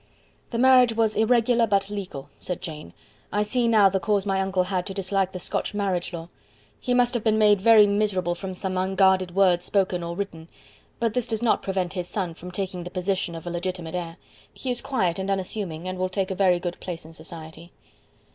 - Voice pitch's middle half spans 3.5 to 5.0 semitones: No, average, 2.8 semitones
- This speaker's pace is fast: Yes, fast, 210 wpm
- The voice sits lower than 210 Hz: Yes, high, 190 Hz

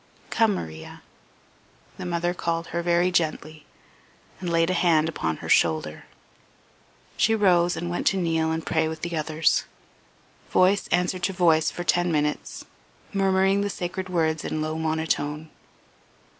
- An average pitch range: No, narrow, 2.2 semitones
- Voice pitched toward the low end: No, medium, 170 Hz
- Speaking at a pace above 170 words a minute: No, average, 145 wpm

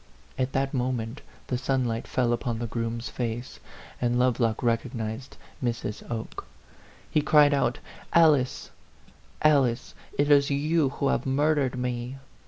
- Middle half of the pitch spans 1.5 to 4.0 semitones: Yes, average, 2.9 semitones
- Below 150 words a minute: Yes, average, 140 wpm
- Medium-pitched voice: No, low, 125 Hz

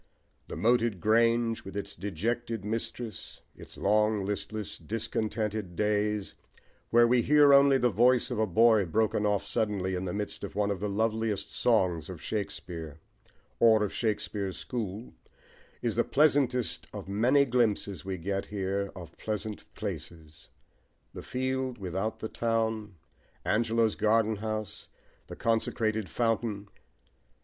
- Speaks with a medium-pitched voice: No, low, 110 Hz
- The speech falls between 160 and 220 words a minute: No, slow, 135 wpm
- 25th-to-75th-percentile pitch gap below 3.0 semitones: Yes, narrow, 2.6 semitones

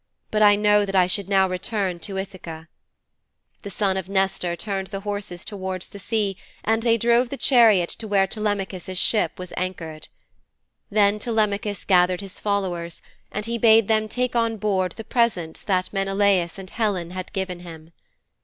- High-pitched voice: Yes, high, 195 Hz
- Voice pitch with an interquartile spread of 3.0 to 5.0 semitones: No, narrow, 2.5 semitones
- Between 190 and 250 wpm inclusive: No, average, 170 wpm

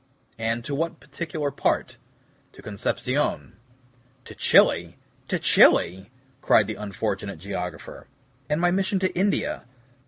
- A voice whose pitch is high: No, low, 125 Hz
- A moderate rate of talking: No, slow, 120 wpm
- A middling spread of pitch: No, wide, 8.7 semitones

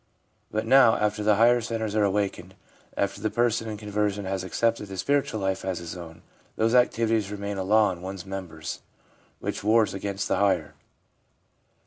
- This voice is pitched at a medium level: No, low, 105 Hz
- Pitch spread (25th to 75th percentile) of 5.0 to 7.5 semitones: No, average, 2.7 semitones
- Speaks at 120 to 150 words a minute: No, average, 170 wpm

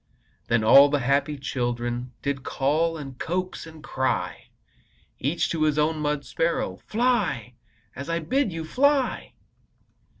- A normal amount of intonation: Yes, average, 3.8 semitones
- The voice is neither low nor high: Yes, medium, 150 Hz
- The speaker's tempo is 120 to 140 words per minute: Yes, slow, 135 wpm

